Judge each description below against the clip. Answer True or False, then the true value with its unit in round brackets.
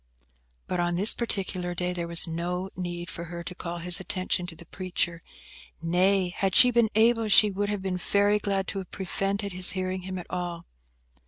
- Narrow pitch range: True (2.1 semitones)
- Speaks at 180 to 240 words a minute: True (195 wpm)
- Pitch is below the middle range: False (185 Hz)